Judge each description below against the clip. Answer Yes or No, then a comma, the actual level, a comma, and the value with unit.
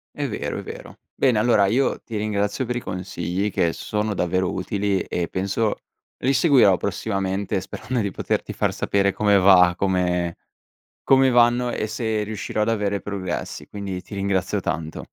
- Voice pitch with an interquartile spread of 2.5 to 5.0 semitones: Yes, average, 2.8 semitones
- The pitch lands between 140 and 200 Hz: No, low, 100 Hz